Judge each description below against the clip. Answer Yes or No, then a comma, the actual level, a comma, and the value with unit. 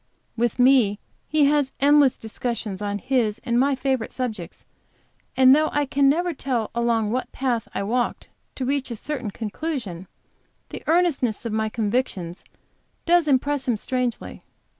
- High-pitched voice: Yes, very high, 250 Hz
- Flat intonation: No, average, 4.1 semitones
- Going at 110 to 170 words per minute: Yes, average, 150 wpm